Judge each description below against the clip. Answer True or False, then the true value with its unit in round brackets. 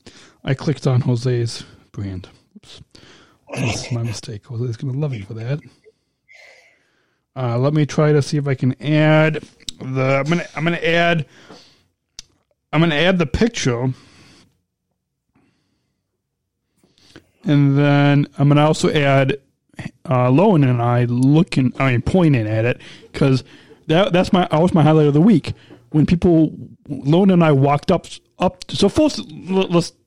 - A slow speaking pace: False (150 wpm)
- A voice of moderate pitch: True (145 Hz)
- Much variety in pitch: False (4.2 semitones)